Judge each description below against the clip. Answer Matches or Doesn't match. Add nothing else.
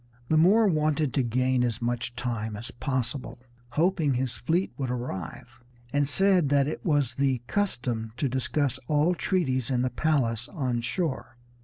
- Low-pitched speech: Matches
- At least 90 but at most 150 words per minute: Doesn't match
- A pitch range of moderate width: Matches